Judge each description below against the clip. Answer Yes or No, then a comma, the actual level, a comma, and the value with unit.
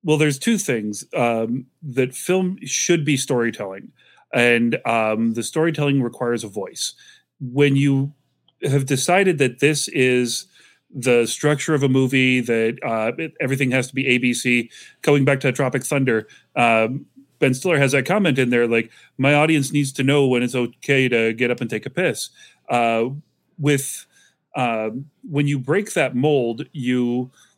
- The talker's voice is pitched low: Yes, low, 130 Hz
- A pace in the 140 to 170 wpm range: Yes, average, 165 wpm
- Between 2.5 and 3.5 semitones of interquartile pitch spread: Yes, average, 3.2 semitones